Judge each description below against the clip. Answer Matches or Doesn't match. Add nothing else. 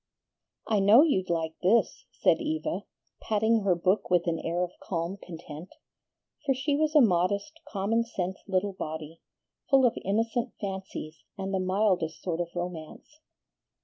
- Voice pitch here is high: Matches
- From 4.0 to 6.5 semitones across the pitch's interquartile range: Matches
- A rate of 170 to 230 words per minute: Doesn't match